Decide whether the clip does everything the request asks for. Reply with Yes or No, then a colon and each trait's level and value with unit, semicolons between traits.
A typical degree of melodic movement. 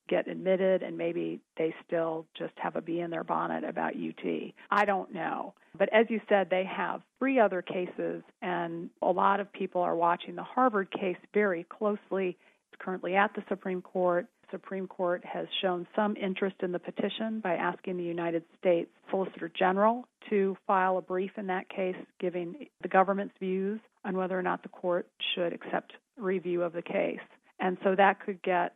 No: narrow, 2.1 semitones